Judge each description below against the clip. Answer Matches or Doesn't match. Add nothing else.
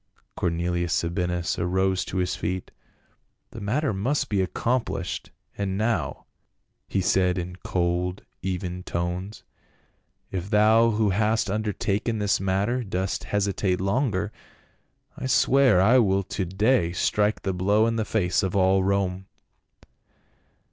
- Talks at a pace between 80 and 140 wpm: Matches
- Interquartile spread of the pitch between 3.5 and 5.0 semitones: Doesn't match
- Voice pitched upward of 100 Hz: Doesn't match